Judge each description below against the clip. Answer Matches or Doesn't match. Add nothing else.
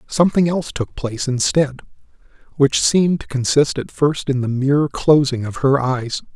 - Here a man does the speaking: Matches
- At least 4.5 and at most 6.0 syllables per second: Matches